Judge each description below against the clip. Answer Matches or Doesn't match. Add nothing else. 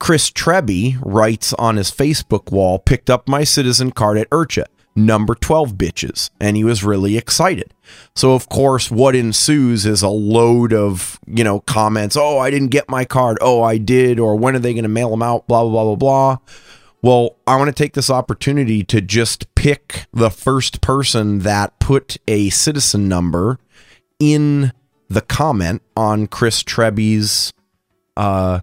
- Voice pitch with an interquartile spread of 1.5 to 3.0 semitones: Doesn't match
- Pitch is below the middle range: Matches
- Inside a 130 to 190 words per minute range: Matches